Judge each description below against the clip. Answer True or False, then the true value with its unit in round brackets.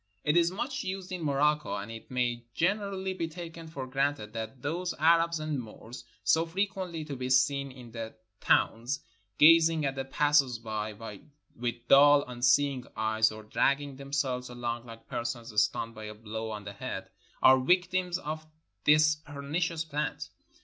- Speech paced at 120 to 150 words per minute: False (165 wpm)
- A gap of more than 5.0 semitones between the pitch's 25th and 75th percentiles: True (5.4 semitones)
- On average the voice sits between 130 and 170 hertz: True (140 Hz)